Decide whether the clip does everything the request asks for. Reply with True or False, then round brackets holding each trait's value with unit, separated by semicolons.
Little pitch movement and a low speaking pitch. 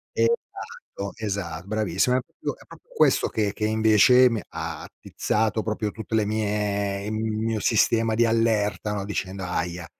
True (1.8 semitones; 110 Hz)